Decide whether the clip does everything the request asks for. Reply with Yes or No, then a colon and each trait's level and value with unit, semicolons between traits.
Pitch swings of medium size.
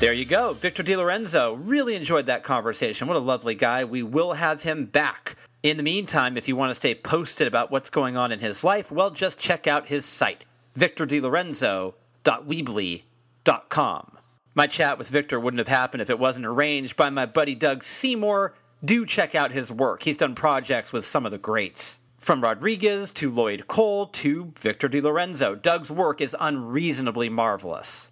No: wide, 5.8 semitones